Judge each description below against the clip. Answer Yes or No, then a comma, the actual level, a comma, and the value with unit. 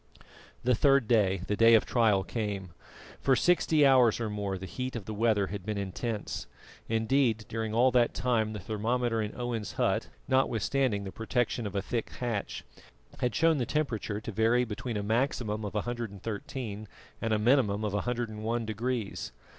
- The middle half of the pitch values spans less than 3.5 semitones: Yes, average, 2.8 semitones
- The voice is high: No, low, 115 Hz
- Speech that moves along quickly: No, average, 170 wpm